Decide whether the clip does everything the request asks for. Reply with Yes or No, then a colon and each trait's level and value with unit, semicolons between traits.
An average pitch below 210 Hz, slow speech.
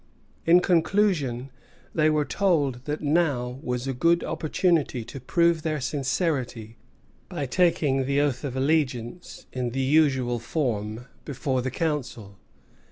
Yes: medium, 140 Hz; slow, 130 wpm